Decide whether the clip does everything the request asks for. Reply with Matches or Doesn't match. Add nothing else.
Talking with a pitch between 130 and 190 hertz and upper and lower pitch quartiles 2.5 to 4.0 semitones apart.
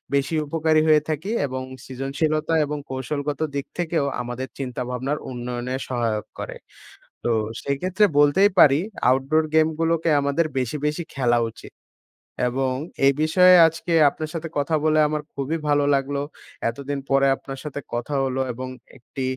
Matches